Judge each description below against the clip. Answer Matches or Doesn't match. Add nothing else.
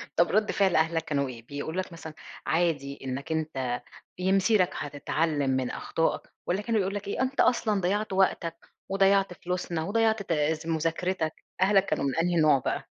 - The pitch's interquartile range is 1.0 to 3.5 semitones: Doesn't match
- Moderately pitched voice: Matches